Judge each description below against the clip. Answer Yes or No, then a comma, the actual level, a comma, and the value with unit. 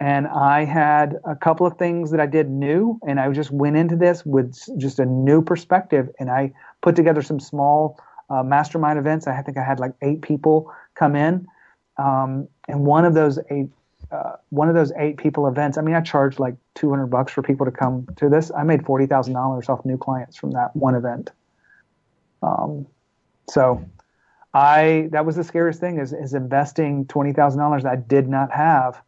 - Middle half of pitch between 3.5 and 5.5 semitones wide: No, narrow, 2.4 semitones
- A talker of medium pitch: Yes, medium, 145 Hz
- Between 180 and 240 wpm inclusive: Yes, average, 190 wpm